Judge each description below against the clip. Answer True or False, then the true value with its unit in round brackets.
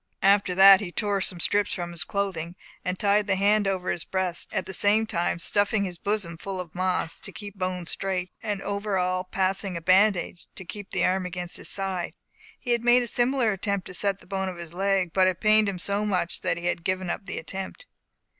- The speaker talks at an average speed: False (230 wpm)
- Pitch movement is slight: True (2.0 semitones)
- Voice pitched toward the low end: False (190 Hz)